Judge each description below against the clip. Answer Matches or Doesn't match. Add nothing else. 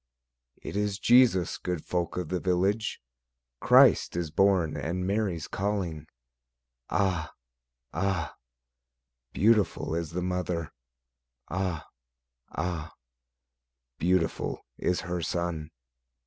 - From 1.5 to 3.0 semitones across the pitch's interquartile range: Matches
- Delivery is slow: Matches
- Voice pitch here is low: Matches